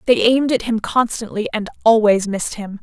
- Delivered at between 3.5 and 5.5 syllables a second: No, 5.7 syllables/s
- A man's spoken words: No, female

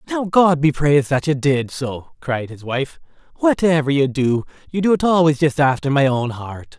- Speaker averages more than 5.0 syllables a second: No, 4.8 syllables/s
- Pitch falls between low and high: Yes, medium, 145 Hz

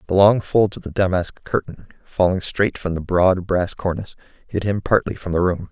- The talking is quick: Yes, fast, 210 wpm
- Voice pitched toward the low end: Yes, very low, 95 Hz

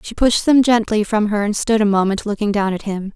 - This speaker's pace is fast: Yes, fast, 265 wpm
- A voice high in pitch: Yes, high, 210 Hz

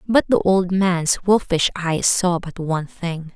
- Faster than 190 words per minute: No, average, 180 wpm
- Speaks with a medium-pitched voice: Yes, medium, 180 Hz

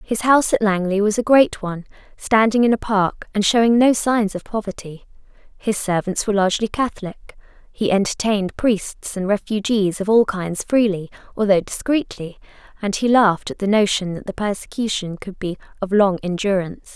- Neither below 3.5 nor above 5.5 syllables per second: Yes, 5.3 syllables/s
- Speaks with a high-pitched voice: Yes, high, 205 Hz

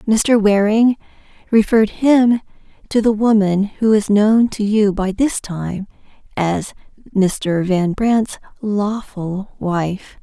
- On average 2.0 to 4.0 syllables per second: Yes, 3.2 syllables/s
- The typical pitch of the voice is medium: No, high, 210 Hz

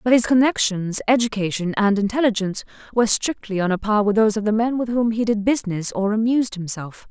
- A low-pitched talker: No, high, 215 Hz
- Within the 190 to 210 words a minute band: Yes, fast, 205 wpm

